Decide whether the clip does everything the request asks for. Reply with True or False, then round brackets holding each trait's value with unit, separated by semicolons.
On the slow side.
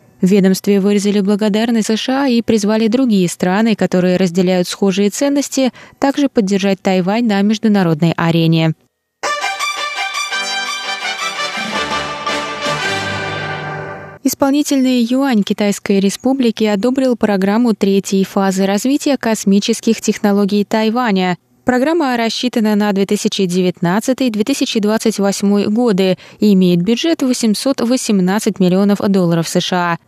True (85 wpm)